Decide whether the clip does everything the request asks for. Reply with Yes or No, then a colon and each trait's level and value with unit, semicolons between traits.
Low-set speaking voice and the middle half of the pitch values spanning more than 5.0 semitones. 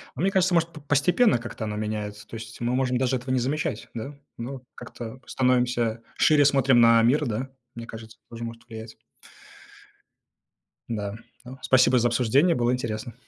No: low, 120 Hz; average, 2.8 semitones